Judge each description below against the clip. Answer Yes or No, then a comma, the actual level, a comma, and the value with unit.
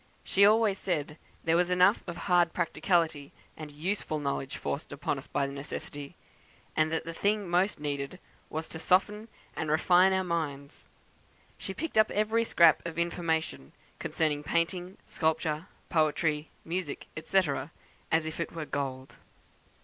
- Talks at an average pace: Yes, average, 145 wpm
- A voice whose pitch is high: No, medium, 165 Hz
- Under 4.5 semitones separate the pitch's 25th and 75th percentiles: Yes, average, 3.3 semitones